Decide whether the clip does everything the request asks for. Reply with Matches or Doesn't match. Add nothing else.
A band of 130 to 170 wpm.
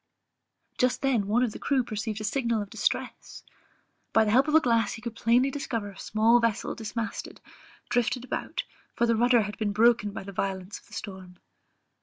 Doesn't match